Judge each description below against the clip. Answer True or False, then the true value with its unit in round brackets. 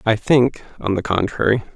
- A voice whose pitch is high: False (110 Hz)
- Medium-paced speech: True (170 wpm)